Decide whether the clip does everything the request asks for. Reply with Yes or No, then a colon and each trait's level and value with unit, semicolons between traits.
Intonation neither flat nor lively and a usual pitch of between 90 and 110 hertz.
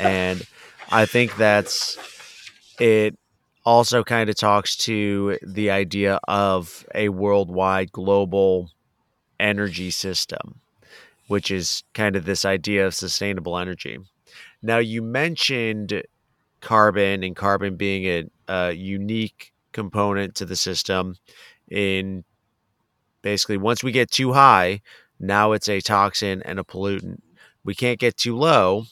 No: narrow, 2.3 semitones; low, 100 Hz